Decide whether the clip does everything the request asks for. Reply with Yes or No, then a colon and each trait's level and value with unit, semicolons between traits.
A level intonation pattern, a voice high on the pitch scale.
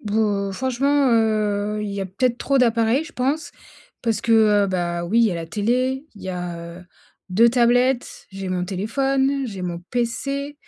No: average, 5.0 semitones; high, 225 Hz